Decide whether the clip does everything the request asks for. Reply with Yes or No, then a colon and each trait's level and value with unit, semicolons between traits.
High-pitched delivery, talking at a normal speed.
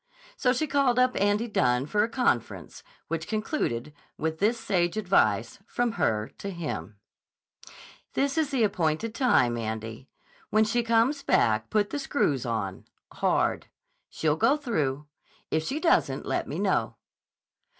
Yes: high, 205 Hz; average, 145 wpm